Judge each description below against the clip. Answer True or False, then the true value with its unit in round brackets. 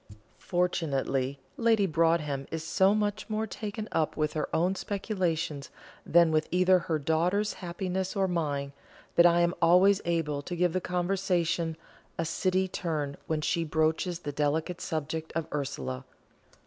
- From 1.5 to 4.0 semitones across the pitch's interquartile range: True (3.1 semitones)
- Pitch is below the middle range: False (170 Hz)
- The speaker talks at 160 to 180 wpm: False (150 wpm)